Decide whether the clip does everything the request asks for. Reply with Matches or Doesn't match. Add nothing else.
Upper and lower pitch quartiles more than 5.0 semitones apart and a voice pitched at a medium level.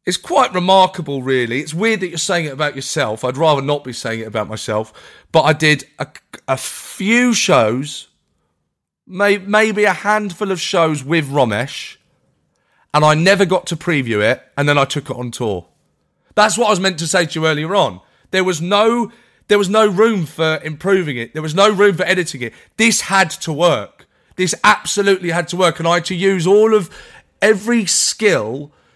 Matches